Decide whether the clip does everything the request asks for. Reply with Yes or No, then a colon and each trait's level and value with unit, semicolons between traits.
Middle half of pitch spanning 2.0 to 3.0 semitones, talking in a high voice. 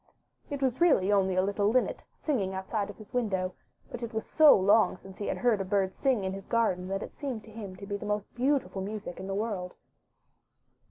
No: average, 3.5 semitones; high, 205 Hz